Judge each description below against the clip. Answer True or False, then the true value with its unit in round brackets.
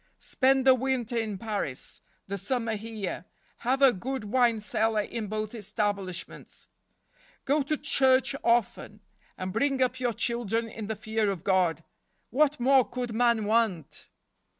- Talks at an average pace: True (145 wpm)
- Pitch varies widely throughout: False (3.8 semitones)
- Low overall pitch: False (225 Hz)